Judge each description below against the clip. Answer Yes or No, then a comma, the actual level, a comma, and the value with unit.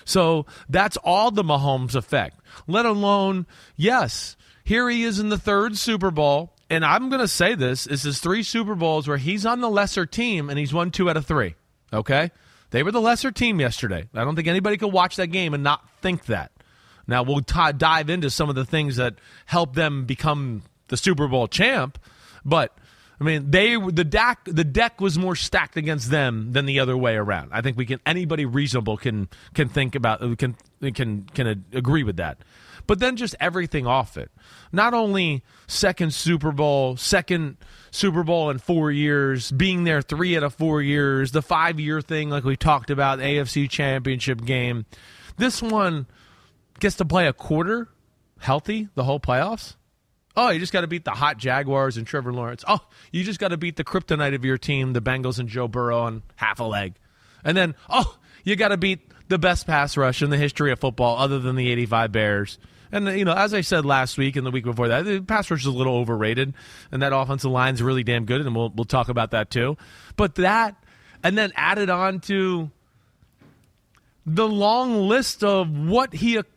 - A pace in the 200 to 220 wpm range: Yes, fast, 205 wpm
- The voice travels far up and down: Yes, wide, 6.4 semitones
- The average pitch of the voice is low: No, medium, 145 Hz